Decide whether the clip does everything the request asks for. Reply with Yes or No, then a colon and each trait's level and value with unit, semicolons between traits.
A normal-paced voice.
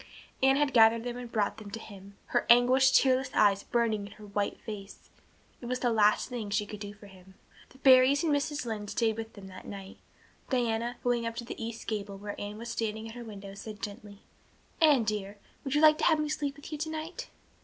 No: fast, 220 wpm